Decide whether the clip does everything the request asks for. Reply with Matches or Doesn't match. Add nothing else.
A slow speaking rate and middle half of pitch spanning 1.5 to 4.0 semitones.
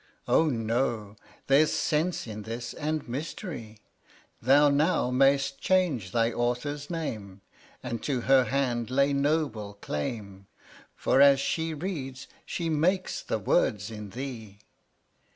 Doesn't match